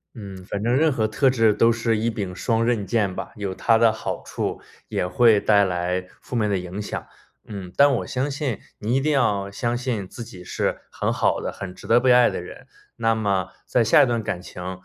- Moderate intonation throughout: Yes, average, 3.6 semitones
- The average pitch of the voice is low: Yes, low, 110 Hz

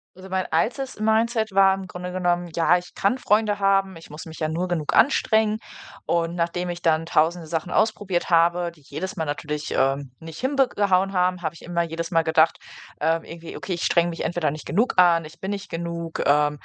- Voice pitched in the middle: Yes, medium, 175 Hz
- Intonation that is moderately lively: Yes, average, 3.0 semitones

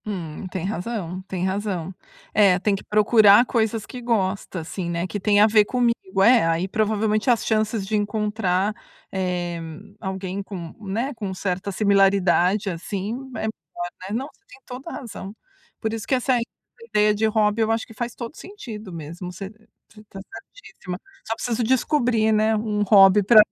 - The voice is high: Yes, high, 210 Hz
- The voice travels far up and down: No, average, 2.9 semitones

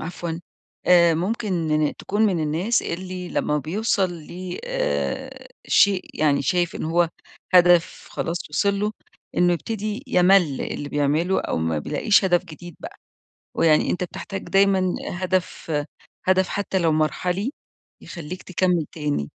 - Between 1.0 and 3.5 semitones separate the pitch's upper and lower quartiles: Yes, average, 2.9 semitones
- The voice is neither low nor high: Yes, medium, 175 Hz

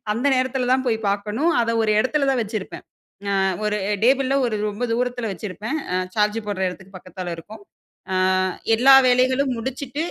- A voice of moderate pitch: No, high, 235 Hz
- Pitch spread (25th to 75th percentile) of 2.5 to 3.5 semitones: No, average, 3.9 semitones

